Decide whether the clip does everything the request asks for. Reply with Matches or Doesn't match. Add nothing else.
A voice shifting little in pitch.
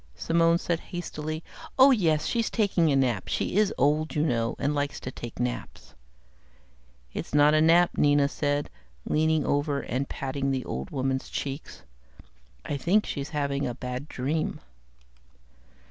Doesn't match